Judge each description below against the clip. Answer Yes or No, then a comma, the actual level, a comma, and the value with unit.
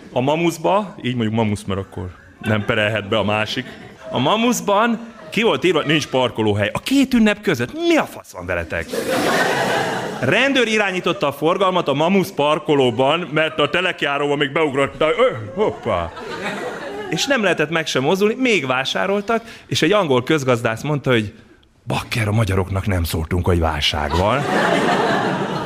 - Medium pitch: Yes, medium, 145 Hz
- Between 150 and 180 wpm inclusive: Yes, fast, 155 wpm